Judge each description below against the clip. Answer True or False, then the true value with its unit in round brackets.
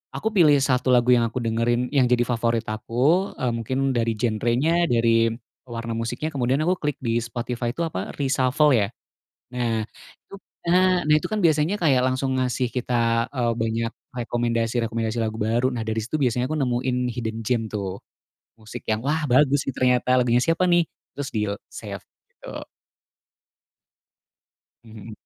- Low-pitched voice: True (120 Hz)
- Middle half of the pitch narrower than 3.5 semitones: True (2.8 semitones)